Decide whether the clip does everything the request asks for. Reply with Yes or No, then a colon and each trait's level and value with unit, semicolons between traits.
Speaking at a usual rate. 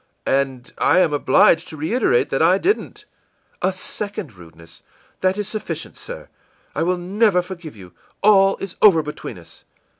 Yes: average, 160 wpm